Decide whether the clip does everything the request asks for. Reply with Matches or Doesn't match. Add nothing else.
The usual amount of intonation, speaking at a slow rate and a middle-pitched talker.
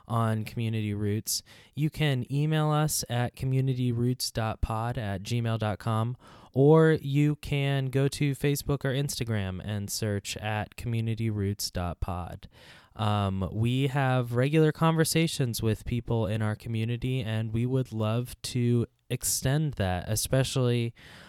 Doesn't match